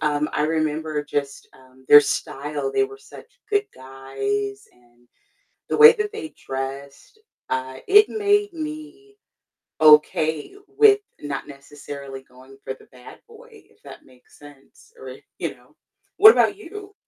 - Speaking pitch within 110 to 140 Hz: No, medium, 150 Hz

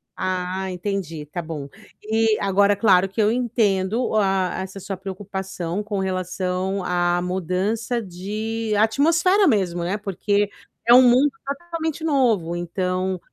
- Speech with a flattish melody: No, average, 3.5 semitones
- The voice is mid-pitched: No, high, 195 Hz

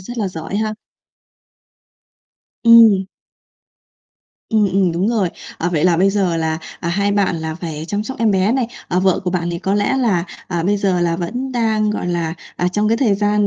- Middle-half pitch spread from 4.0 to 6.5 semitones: No, average, 3.6 semitones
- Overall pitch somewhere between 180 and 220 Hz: Yes, high, 195 Hz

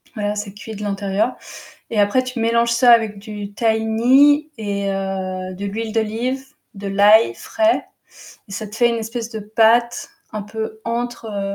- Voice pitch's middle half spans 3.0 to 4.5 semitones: No, narrow, 2.4 semitones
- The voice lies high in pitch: Yes, high, 220 Hz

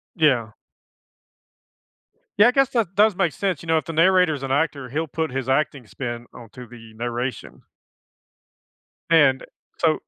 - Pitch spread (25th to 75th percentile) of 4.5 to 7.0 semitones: Yes, average, 5.2 semitones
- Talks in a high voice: No, medium, 145 Hz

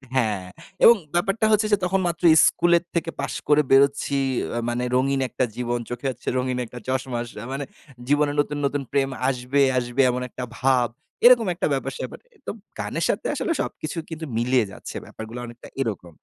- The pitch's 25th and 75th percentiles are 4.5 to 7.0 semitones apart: No, average, 3.8 semitones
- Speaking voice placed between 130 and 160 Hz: Yes, low, 135 Hz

